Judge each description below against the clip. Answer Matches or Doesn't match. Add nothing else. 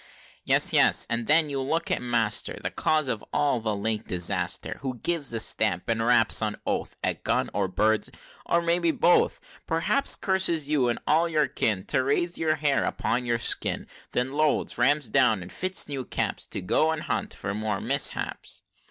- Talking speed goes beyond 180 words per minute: Matches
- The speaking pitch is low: Matches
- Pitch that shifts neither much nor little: Doesn't match